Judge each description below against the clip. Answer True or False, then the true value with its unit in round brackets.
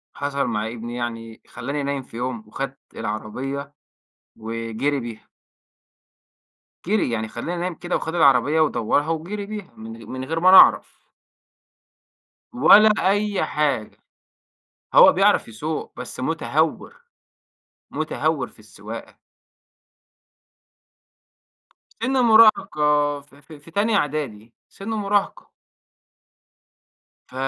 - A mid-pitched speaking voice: True (145 Hz)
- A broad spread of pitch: True (7.1 semitones)